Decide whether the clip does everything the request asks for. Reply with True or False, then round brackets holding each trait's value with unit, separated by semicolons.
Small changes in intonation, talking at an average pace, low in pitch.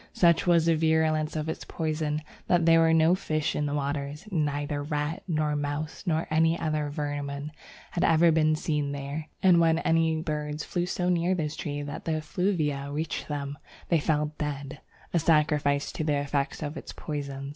False (2.0 semitones; 180 wpm; 155 Hz)